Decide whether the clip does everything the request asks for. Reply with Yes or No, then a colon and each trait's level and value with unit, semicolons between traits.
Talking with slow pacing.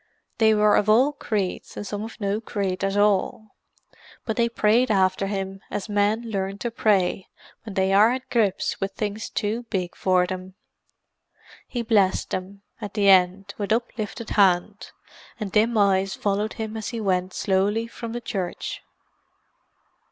No: average, 160 wpm